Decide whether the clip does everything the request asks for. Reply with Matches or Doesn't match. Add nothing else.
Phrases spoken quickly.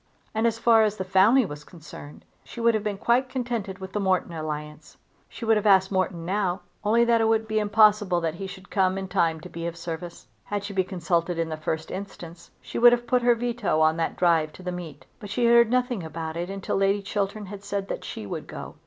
Matches